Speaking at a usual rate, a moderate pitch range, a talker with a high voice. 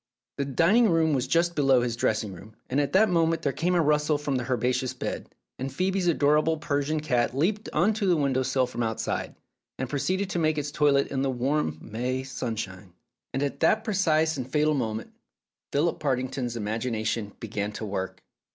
No: average, 190 wpm; average, 4.7 semitones; medium, 140 Hz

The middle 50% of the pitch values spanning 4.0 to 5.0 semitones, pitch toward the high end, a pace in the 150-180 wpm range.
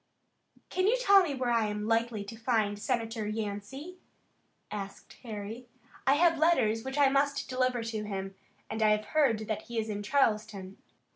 Yes: average, 4.3 semitones; high, 225 Hz; average, 170 wpm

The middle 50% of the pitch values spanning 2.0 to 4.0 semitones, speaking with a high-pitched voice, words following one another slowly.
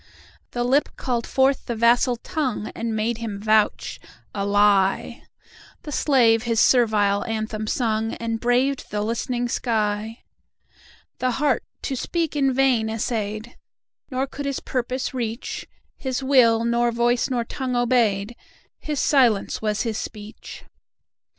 Yes: average, 2.8 semitones; high, 235 Hz; slow, 110 wpm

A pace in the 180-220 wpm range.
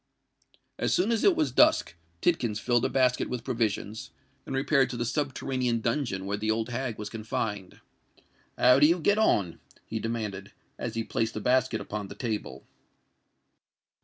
No: average, 165 wpm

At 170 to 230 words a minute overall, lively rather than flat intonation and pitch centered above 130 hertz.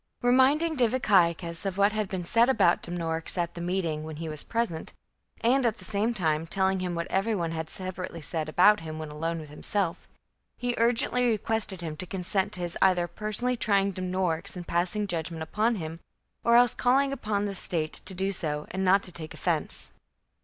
No: average, 200 wpm; average, 4.4 semitones; medium, 185 Hz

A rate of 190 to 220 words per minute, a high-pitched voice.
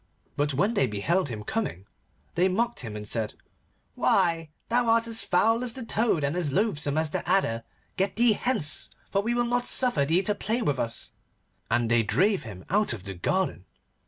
No: average, 195 wpm; medium, 180 Hz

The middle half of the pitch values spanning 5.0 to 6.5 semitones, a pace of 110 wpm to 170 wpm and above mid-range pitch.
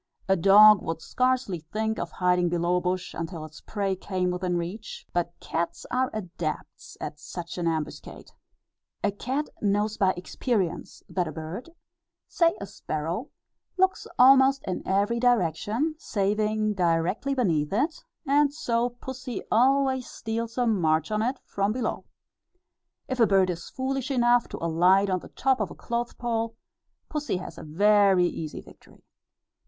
Yes: wide, 5.6 semitones; average, 150 wpm; high, 205 Hz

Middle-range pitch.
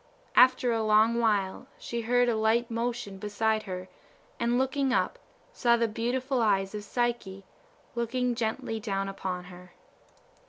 No: high, 225 Hz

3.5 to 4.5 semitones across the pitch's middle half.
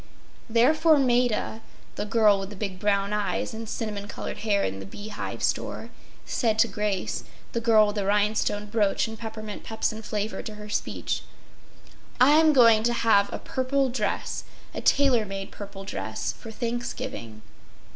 No: narrow, 2.4 semitones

